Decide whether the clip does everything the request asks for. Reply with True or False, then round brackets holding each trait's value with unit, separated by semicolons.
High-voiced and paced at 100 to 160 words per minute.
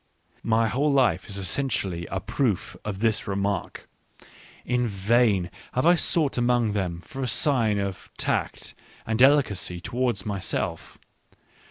False (110 Hz; 140 wpm)